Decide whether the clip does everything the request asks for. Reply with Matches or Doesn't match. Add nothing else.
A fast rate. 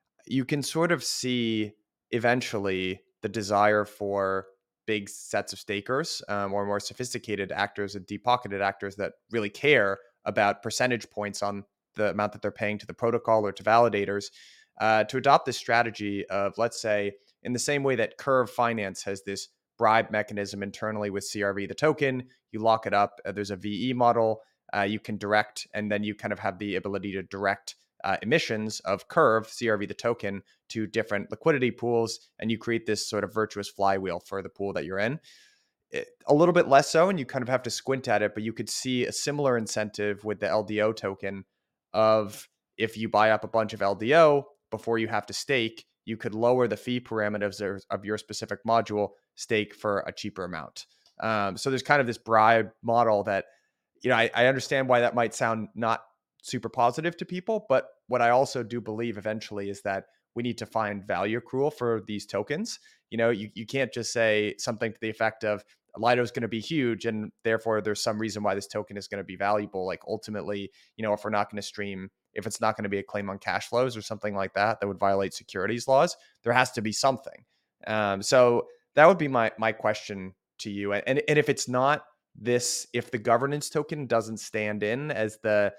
Matches